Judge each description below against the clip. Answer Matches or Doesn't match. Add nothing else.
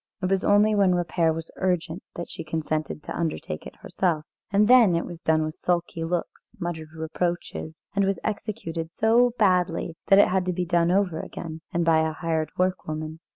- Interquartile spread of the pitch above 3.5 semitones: Doesn't match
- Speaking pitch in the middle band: Matches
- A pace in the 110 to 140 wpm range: Doesn't match